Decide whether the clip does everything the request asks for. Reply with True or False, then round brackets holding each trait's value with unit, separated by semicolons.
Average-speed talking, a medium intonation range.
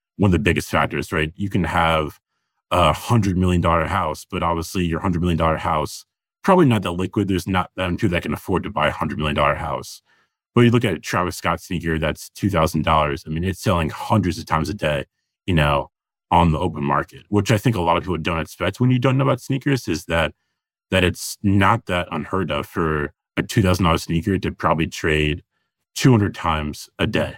False (230 wpm; 3.9 semitones)